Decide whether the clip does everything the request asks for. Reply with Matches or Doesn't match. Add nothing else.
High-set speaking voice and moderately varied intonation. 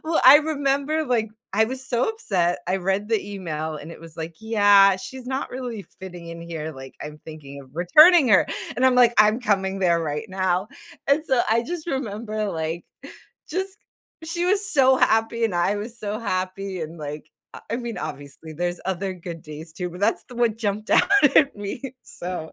Doesn't match